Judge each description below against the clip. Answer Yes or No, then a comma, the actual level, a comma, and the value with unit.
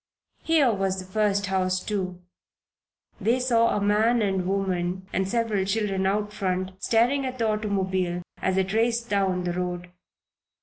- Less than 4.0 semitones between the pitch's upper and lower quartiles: Yes, average, 3.0 semitones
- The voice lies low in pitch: No, high, 195 Hz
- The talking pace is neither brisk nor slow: Yes, average, 150 wpm